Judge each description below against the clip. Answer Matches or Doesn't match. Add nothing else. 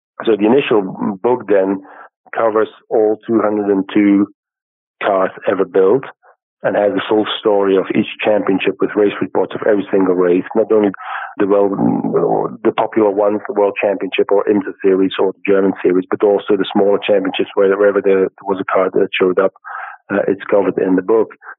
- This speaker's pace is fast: Doesn't match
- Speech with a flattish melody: Matches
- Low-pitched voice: Matches